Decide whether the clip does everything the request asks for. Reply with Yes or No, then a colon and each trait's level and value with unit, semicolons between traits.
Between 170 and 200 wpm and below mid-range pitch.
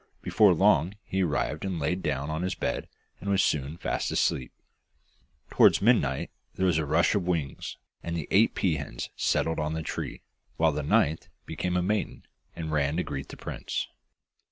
Yes: average, 180 wpm; very low, 80 Hz